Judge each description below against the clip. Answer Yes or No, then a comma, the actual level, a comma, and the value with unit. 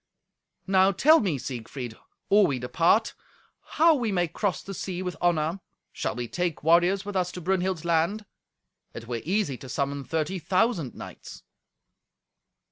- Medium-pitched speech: Yes, medium, 175 Hz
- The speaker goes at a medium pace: Yes, average, 150 wpm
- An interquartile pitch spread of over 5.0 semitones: No, average, 4.7 semitones